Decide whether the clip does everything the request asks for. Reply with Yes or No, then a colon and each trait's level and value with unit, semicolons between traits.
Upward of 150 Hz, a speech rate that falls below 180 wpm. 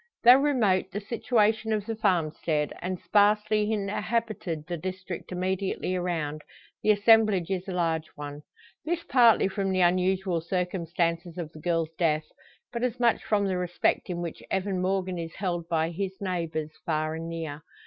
Yes: medium, 185 Hz; average, 165 wpm